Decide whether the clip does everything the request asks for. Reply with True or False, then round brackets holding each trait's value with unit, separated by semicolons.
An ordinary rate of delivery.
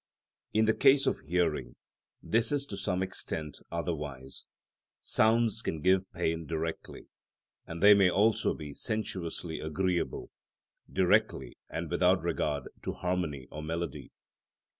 False (125 wpm)